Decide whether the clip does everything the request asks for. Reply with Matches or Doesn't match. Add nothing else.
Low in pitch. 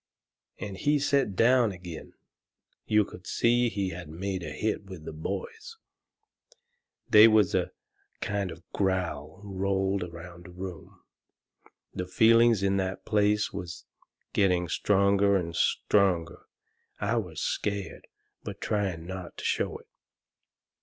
Matches